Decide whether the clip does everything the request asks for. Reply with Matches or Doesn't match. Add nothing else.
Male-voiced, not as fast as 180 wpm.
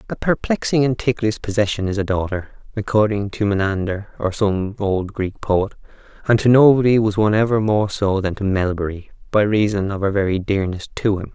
Doesn't match